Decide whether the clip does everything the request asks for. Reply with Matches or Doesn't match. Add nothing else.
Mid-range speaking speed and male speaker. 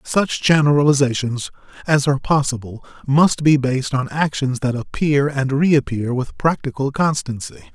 Doesn't match